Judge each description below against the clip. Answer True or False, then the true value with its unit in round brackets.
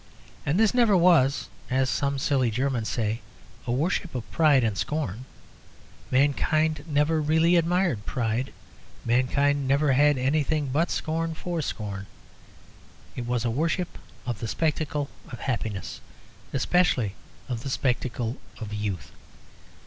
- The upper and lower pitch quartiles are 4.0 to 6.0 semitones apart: True (4.7 semitones)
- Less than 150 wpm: True (135 wpm)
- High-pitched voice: False (140 Hz)